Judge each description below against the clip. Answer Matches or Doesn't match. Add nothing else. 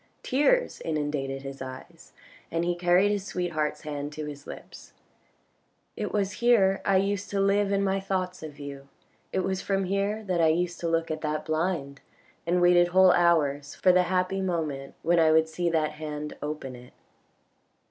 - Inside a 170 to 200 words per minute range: Matches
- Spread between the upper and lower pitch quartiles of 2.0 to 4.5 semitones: Matches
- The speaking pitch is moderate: Matches